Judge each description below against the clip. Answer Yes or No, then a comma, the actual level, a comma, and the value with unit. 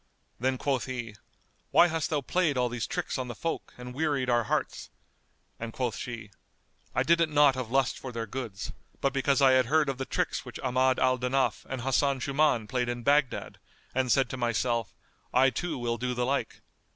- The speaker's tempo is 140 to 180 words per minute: No, average, 200 wpm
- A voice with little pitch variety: Yes, narrow, 2.3 semitones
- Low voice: Yes, low, 130 Hz